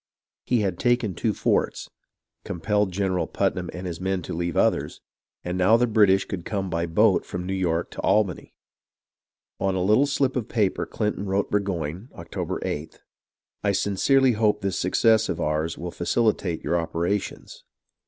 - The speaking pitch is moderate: No, very low, 95 Hz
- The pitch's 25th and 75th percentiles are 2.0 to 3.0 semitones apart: No, average, 3.4 semitones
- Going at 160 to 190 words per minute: Yes, average, 170 wpm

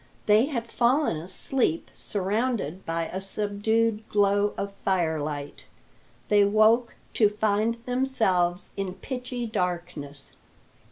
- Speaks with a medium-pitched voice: No, high, 205 Hz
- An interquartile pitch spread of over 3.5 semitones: Yes, average, 4.2 semitones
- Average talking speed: No, slow, 105 wpm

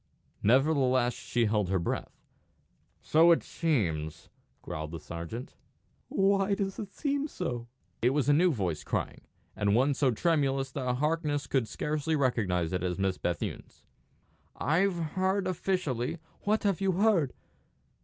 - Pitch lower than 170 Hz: Yes, medium, 140 Hz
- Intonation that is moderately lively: No, wide, 8.0 semitones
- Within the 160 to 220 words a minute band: No, average, 145 wpm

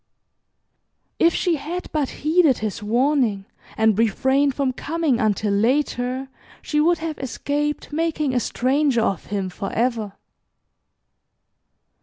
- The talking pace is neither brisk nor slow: No, slow, 115 wpm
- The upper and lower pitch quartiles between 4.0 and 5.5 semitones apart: Yes, average, 5.1 semitones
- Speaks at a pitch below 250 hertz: No, very high, 265 Hz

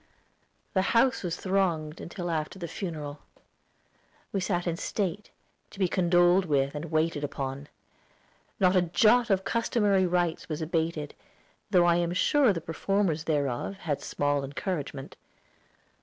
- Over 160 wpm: No, average, 140 wpm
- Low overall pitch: No, medium, 175 Hz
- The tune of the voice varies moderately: Yes, average, 3.9 semitones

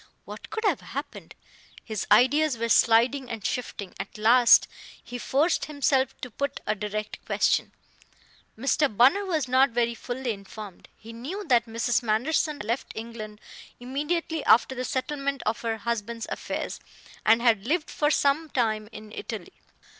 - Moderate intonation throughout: Yes, average, 4.0 semitones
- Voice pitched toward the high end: Yes, high, 240 Hz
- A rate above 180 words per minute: No, average, 155 wpm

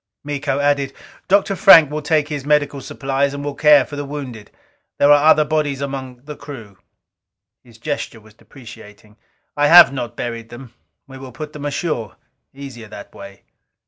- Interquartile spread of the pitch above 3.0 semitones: Yes, average, 3.4 semitones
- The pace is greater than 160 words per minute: Yes, average, 170 wpm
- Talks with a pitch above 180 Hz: No, medium, 140 Hz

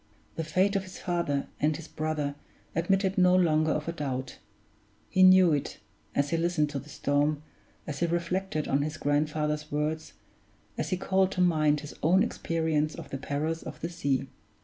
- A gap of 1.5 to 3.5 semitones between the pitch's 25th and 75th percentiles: Yes, average, 2.9 semitones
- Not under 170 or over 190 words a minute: Yes, average, 180 wpm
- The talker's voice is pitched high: No, medium, 155 Hz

